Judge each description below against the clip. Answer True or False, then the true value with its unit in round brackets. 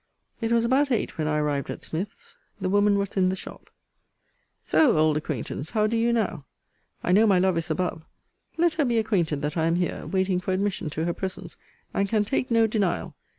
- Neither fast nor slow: False (210 wpm)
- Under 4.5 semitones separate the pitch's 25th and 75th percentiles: False (5.2 semitones)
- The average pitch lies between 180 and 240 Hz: True (190 Hz)